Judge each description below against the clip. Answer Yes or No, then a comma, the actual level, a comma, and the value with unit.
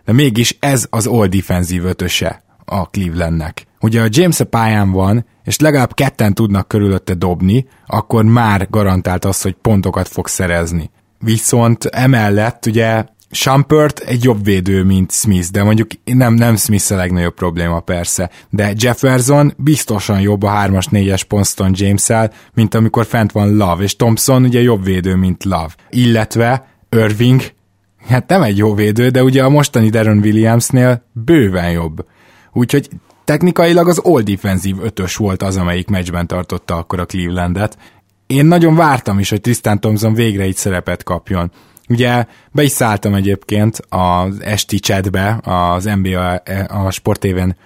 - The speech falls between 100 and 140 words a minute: No, average, 150 wpm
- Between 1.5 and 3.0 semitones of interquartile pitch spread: No, average, 4.1 semitones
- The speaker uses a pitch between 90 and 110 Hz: Yes, low, 105 Hz